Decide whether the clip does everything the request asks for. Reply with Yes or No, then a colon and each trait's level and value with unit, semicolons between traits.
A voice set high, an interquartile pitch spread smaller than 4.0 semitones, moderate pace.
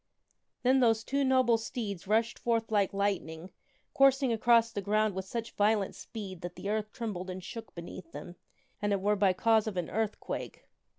Yes: high, 210 Hz; average, 3.1 semitones; average, 180 wpm